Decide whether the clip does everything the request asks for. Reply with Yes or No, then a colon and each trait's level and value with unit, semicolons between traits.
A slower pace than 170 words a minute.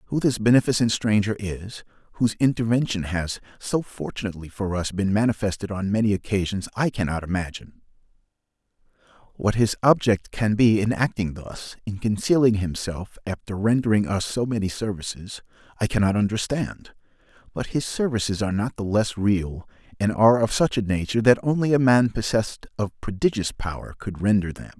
Yes: average, 155 wpm